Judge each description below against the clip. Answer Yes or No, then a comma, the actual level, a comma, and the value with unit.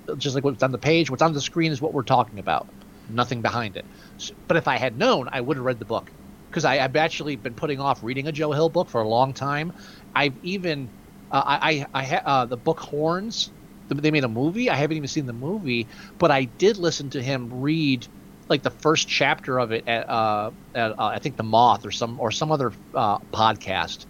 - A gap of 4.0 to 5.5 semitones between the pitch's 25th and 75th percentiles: Yes, average, 4.6 semitones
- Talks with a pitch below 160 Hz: Yes, medium, 140 Hz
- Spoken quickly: Yes, fast, 230 wpm